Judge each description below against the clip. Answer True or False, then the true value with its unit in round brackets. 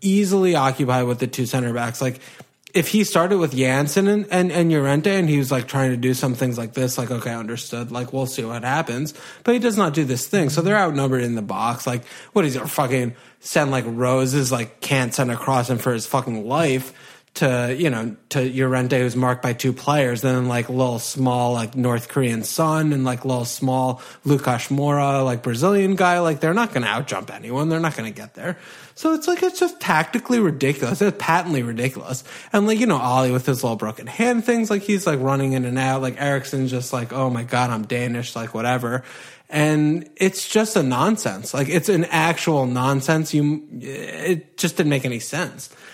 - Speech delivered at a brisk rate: True (210 wpm)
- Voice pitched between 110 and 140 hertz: True (135 Hz)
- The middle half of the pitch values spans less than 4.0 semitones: False (4.6 semitones)